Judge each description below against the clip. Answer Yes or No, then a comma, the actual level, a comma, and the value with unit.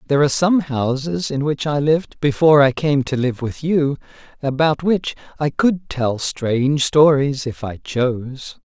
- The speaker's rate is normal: Yes, average, 175 wpm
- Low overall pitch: No, medium, 145 Hz